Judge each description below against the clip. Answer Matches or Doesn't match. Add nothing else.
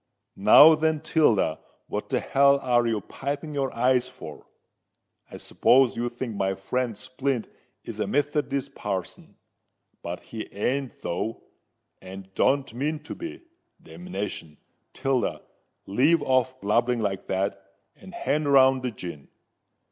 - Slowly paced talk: Matches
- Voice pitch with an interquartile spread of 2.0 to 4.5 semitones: Doesn't match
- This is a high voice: Doesn't match